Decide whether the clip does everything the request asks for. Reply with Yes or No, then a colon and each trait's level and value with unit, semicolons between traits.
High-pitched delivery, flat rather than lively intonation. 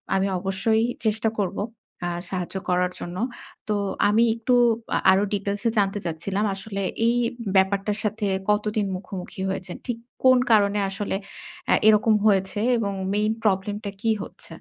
Yes: high, 205 Hz; narrow, 1.9 semitones